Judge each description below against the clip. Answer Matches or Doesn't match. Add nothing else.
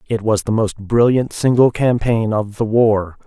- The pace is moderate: Matches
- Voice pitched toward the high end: Doesn't match